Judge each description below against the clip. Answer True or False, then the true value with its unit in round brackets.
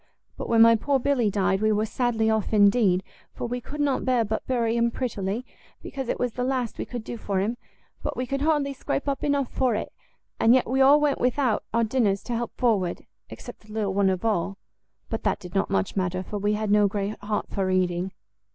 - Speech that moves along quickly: True (225 wpm)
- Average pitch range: True (4.0 semitones)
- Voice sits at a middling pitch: False (225 Hz)